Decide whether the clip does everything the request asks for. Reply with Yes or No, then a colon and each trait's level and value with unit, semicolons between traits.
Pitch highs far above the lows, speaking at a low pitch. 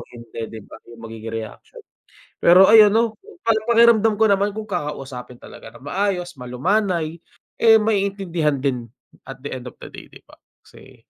No: wide, 8.8 semitones; medium, 175 Hz